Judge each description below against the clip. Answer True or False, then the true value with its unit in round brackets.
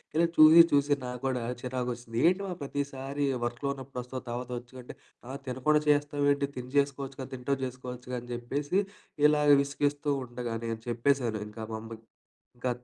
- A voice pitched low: True (130 Hz)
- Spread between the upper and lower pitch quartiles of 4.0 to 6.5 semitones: False (2.7 semitones)